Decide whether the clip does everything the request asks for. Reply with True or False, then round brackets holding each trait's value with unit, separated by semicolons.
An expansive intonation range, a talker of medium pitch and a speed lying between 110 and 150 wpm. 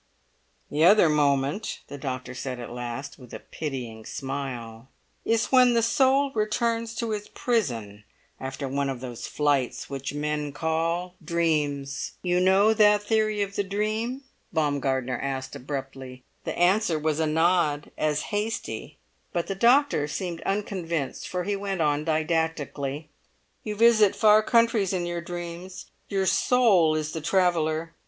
True (6.5 semitones; 165 Hz; 145 wpm)